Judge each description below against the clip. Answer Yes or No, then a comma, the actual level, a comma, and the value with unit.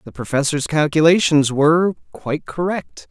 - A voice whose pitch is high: No, medium, 150 Hz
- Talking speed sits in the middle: No, slow, 115 wpm